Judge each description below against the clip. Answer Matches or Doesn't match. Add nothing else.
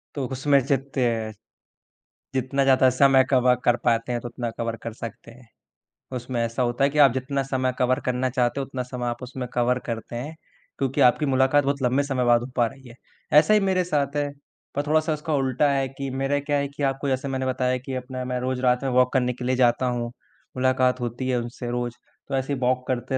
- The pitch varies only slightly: Matches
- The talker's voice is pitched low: Matches